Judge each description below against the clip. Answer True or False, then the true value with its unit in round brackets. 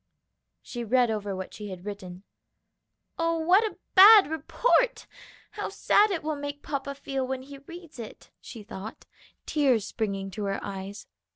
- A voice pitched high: True (260 Hz)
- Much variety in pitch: True (7.6 semitones)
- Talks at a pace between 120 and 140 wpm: False (160 wpm)